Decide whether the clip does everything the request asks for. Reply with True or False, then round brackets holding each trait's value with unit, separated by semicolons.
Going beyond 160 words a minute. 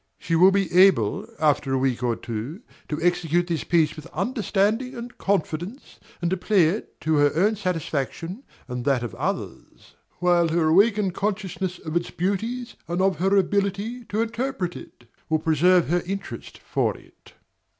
True (170 wpm)